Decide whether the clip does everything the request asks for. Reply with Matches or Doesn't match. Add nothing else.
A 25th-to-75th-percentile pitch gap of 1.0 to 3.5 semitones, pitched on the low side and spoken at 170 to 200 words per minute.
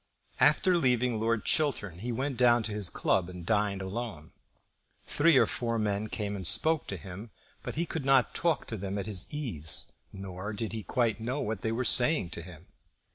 Doesn't match